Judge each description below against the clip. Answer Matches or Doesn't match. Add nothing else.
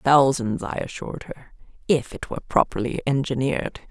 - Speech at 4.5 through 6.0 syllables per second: Matches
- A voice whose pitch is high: Doesn't match